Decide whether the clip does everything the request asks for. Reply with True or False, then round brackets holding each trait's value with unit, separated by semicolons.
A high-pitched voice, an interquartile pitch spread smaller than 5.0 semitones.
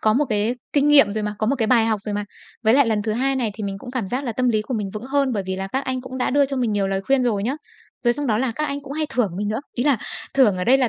True (240 Hz; 4.0 semitones)